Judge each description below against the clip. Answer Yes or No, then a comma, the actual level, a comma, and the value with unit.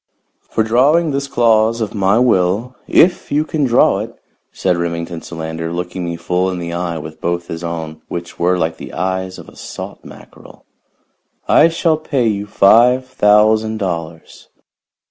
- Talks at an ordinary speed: Yes, average, 165 wpm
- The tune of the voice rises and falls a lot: Yes, wide, 5.7 semitones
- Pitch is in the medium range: No, very low, 95 Hz